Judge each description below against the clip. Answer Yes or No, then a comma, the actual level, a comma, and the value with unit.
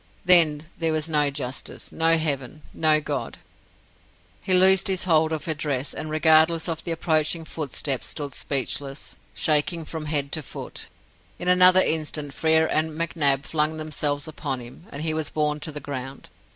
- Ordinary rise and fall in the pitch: No, narrow, 2.0 semitones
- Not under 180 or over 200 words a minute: No, average, 165 wpm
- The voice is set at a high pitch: No, medium, 155 Hz